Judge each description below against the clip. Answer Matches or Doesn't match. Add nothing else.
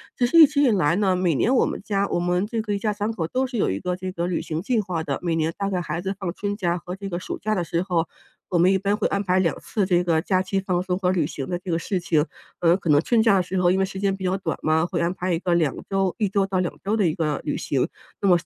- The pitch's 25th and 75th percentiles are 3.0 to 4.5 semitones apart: Doesn't match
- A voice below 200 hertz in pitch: Matches